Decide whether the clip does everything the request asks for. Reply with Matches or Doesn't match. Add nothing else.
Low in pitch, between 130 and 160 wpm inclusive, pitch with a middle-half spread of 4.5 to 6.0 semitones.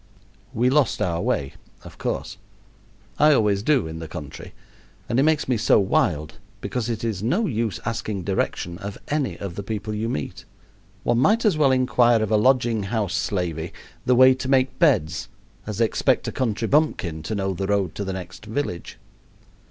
Doesn't match